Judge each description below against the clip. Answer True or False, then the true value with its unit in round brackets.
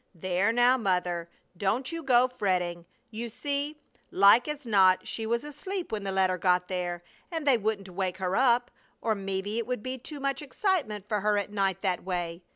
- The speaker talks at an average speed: True (190 wpm)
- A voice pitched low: False (210 Hz)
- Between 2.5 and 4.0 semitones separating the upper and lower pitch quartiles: False (5.3 semitones)